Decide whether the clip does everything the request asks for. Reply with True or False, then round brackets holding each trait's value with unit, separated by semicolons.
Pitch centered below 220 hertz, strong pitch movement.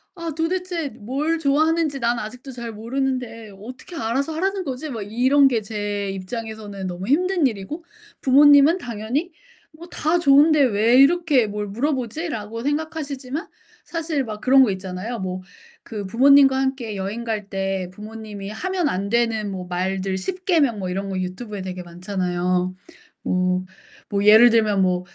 False (230 Hz; 6.2 semitones)